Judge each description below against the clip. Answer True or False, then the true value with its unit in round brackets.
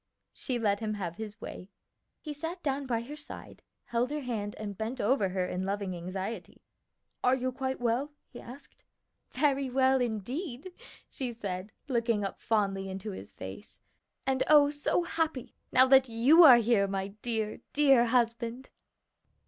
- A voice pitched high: True (240 Hz)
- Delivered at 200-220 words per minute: False (160 wpm)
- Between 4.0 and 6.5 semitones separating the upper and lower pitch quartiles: True (4.4 semitones)